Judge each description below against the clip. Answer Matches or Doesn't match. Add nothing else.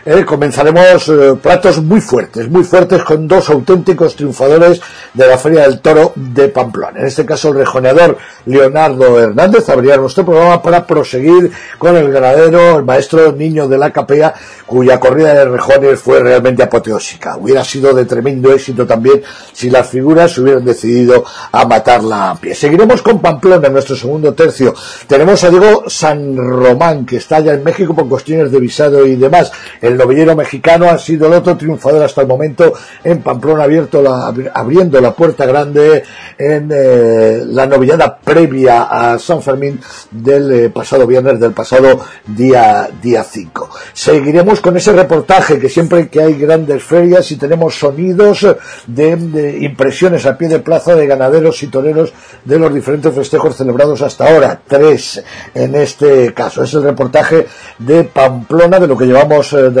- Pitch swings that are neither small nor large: Matches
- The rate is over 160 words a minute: Matches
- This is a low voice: Doesn't match